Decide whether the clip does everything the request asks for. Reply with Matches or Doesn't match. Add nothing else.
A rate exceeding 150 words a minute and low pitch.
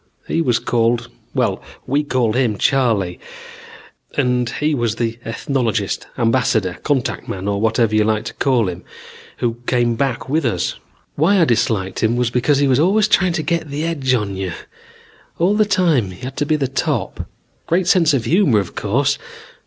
Matches